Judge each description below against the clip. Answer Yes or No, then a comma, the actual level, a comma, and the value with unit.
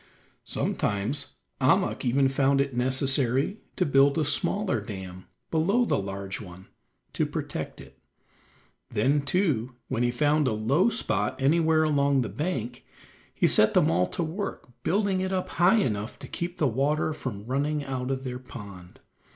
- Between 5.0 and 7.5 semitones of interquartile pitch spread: Yes, wide, 5.5 semitones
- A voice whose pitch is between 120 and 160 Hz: Yes, low, 135 Hz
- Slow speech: No, average, 160 wpm